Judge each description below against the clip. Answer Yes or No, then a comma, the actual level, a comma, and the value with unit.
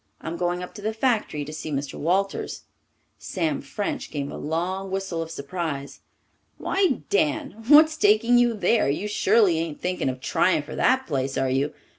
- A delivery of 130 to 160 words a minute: No, average, 175 wpm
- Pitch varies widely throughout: Yes, wide, 6.2 semitones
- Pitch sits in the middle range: Yes, medium, 180 Hz